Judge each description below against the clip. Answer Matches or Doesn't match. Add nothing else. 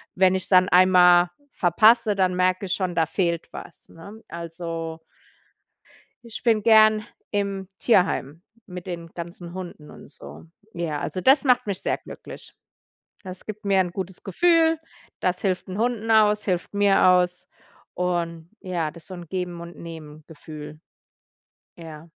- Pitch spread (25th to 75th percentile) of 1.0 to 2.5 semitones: Doesn't match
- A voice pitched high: Doesn't match